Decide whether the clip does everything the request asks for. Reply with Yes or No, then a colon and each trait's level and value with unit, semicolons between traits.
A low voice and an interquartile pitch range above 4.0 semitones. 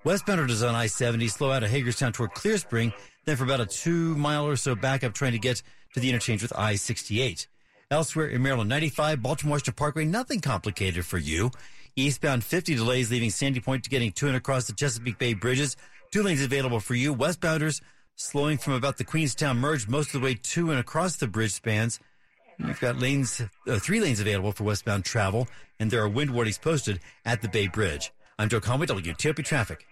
Yes: low, 125 Hz; average, 4.6 semitones